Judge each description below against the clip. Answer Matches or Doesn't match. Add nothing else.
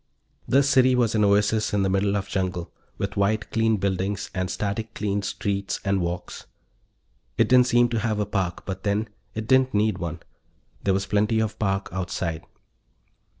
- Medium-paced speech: Matches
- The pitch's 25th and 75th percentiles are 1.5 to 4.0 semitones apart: Matches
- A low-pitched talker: Matches